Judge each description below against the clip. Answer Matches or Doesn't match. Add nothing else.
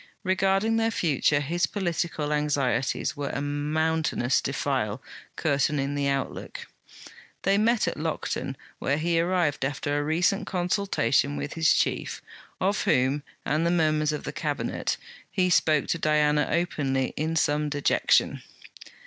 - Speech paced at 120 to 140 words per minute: Matches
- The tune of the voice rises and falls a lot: Doesn't match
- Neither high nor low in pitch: Matches